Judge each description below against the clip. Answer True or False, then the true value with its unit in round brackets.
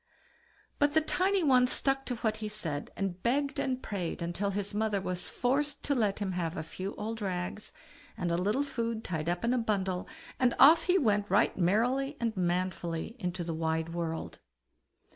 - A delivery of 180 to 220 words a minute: True (185 wpm)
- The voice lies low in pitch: False (205 Hz)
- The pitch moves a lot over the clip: True (6.0 semitones)